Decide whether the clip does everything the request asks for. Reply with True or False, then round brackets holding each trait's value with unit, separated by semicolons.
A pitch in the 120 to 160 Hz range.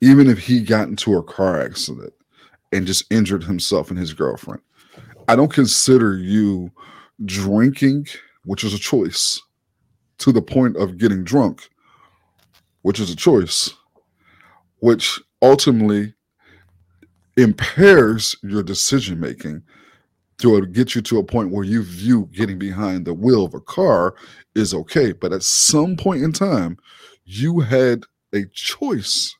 False (105 Hz)